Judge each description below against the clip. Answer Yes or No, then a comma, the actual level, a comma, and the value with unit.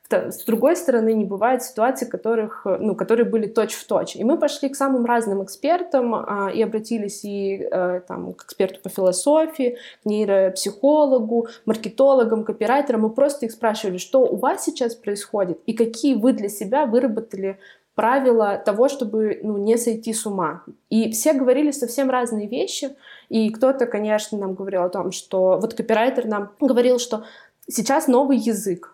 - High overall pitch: Yes, high, 225 Hz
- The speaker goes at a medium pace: No, fast, 165 wpm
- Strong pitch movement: No, average, 4.0 semitones